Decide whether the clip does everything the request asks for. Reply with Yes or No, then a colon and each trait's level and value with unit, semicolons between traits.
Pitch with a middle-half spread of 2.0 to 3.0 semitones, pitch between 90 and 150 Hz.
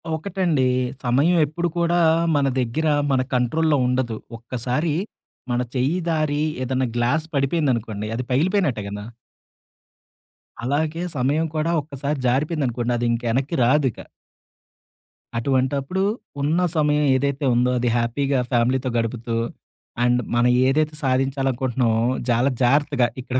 No: average, 3.7 semitones; low, 135 Hz